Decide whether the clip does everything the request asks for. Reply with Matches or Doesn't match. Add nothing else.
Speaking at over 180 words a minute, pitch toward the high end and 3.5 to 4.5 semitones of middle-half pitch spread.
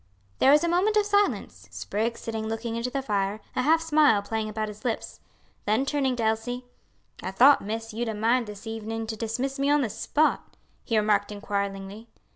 Matches